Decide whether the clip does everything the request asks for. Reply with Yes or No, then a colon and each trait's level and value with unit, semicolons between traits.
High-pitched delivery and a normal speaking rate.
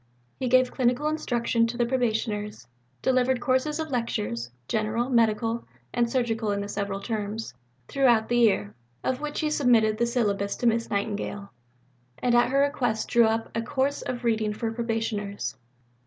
Yes: high, 230 Hz; average, 160 wpm